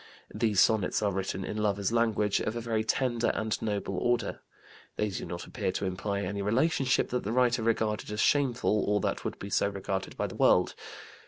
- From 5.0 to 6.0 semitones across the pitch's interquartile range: No, average, 2.7 semitones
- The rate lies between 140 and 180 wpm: No, average, 195 wpm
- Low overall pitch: Yes, low, 105 Hz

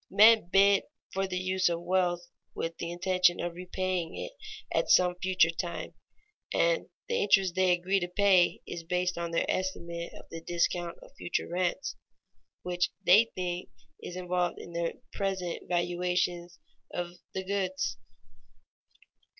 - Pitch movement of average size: No, narrow, 1.4 semitones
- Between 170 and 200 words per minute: No, average, 145 wpm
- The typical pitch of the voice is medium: Yes, medium, 180 Hz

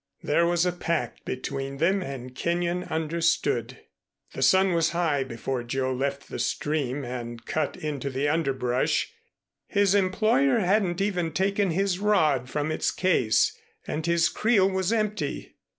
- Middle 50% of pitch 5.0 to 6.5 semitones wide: Yes, wide, 5.6 semitones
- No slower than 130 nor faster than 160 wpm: Yes, average, 145 wpm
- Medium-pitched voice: Yes, medium, 165 Hz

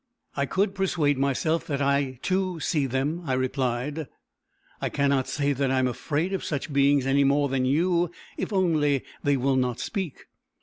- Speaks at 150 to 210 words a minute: Yes, average, 175 wpm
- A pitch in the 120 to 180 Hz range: Yes, medium, 140 Hz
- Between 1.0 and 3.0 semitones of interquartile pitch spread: No, average, 3.4 semitones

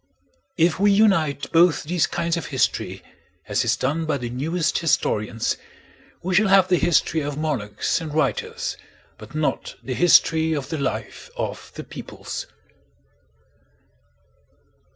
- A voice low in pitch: No, medium, 160 Hz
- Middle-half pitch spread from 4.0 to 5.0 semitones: No, average, 3.6 semitones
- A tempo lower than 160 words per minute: Yes, slow, 135 wpm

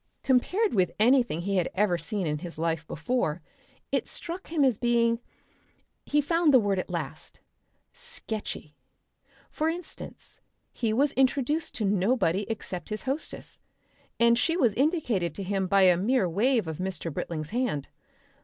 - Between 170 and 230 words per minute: No, average, 155 wpm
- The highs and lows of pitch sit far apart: Yes, wide, 6.6 semitones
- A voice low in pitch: No, high, 220 Hz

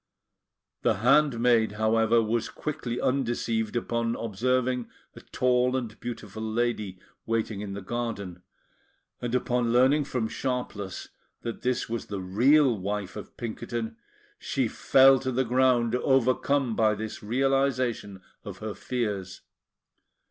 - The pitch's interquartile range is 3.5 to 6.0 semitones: No, average, 2.7 semitones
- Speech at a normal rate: No, slow, 125 wpm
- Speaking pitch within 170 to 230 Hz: No, low, 120 Hz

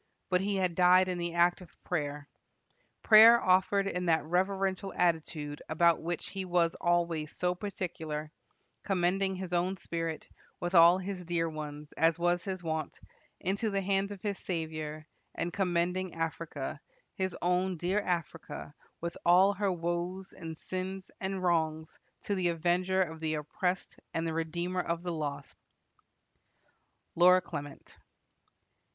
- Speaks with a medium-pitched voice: Yes, medium, 175 Hz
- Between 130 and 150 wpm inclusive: Yes, average, 145 wpm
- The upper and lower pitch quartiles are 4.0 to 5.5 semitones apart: No, narrow, 2.4 semitones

